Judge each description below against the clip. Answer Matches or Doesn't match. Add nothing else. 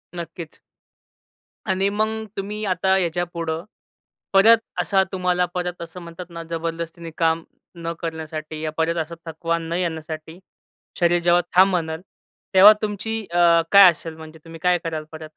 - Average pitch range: Doesn't match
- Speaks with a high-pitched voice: Doesn't match